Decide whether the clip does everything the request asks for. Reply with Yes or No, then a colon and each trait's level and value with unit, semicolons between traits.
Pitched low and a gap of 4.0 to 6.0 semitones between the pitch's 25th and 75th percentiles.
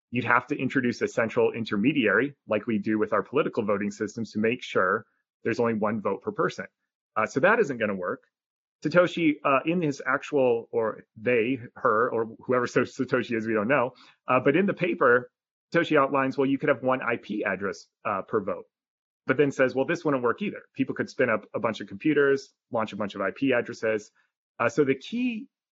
Yes: low, 130 Hz; average, 4.8 semitones